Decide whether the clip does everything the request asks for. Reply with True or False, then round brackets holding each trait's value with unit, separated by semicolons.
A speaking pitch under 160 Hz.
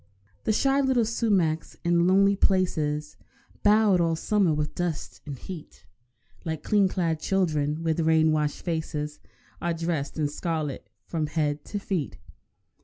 False (165 Hz)